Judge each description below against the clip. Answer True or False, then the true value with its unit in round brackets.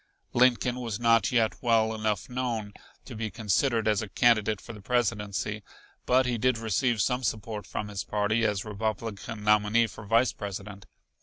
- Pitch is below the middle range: True (110 Hz)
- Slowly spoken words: False (165 wpm)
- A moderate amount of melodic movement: False (2.1 semitones)